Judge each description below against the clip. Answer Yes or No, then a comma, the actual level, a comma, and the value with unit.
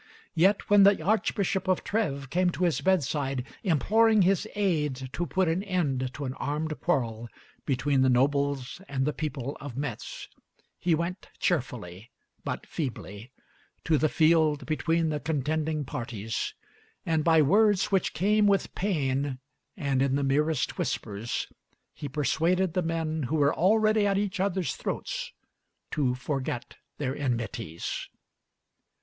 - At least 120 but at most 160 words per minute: Yes, average, 140 wpm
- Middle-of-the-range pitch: Yes, medium, 155 Hz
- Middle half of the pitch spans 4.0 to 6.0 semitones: Yes, wide, 5.4 semitones